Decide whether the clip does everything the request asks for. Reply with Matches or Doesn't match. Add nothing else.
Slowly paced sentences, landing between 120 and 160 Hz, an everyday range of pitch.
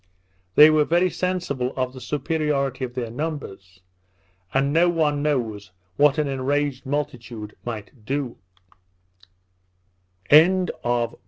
Matches